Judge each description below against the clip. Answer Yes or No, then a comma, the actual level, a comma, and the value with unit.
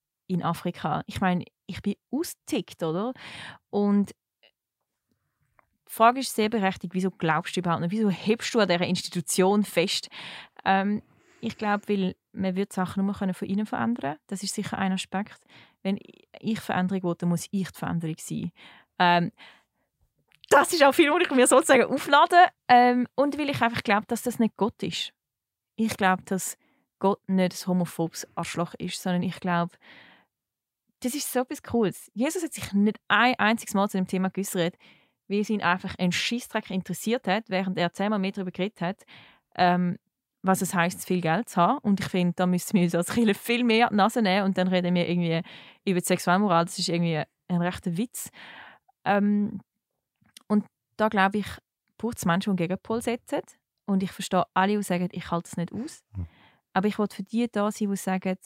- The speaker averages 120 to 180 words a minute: No, fast, 190 wpm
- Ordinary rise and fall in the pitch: Yes, average, 3.5 semitones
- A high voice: Yes, high, 195 Hz